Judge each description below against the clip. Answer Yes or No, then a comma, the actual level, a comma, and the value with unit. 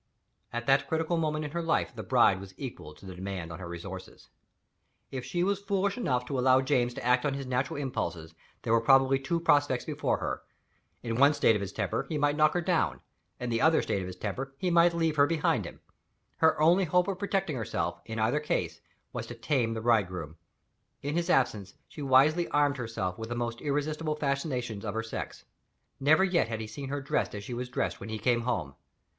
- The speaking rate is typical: No, fast, 215 wpm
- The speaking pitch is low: Yes, low, 130 Hz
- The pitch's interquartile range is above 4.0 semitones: Yes, wide, 5.4 semitones